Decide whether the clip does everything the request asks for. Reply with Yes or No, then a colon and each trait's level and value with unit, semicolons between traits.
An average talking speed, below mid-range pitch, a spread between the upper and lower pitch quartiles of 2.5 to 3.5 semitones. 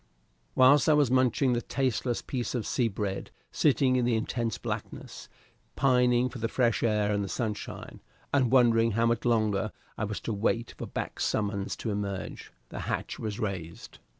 Yes: average, 175 wpm; low, 115 Hz; average, 3.1 semitones